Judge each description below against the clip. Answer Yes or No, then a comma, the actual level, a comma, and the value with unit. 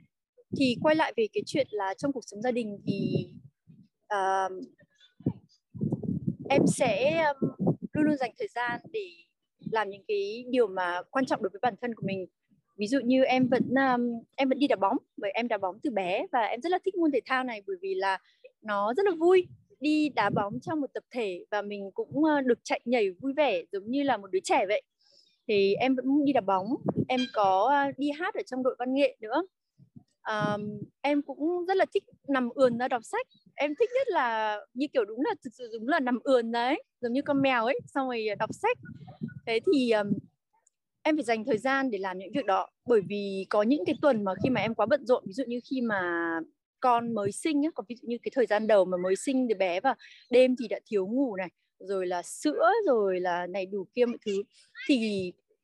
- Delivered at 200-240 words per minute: Yes, average, 225 wpm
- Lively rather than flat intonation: Yes, wide, 6.0 semitones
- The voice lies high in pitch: Yes, very high, 250 Hz